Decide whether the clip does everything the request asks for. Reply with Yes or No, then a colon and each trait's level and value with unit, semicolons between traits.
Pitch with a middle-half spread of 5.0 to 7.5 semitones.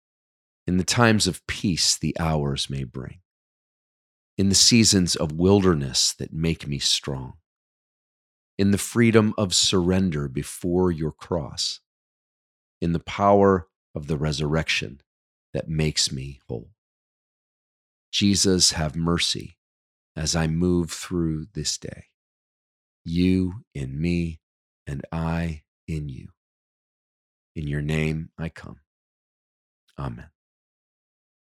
No: average, 4.5 semitones